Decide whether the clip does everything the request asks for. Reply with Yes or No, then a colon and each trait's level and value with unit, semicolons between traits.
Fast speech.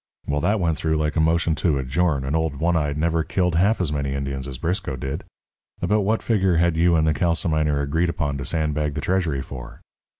Yes: fast, 220 wpm